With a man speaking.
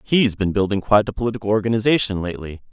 Yes: male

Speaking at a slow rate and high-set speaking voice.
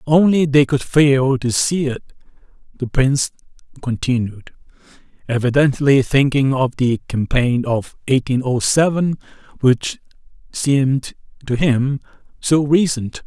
No: slow, 115 wpm; low, 135 Hz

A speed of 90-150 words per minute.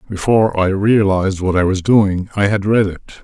No: fast, 205 wpm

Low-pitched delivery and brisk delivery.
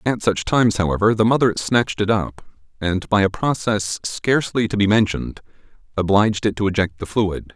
No: low, 105 Hz; average, 185 wpm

